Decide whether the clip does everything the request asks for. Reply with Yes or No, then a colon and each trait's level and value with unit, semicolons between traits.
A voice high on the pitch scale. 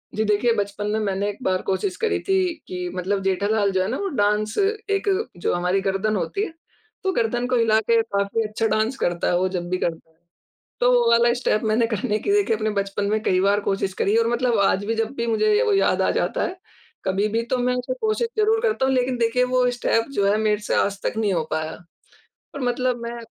Yes: high, 220 Hz